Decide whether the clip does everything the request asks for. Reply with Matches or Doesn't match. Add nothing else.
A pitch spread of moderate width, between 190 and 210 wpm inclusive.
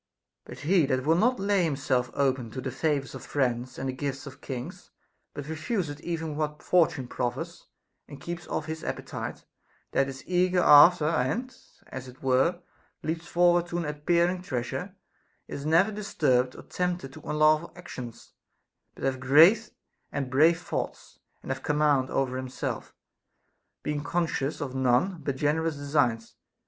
Doesn't match